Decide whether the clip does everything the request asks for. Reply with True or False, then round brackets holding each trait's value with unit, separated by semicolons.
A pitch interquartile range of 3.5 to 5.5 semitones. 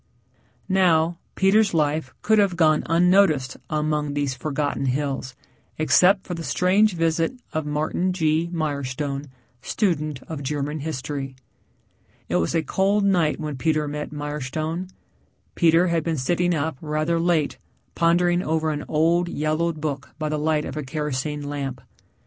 False (2.6 semitones)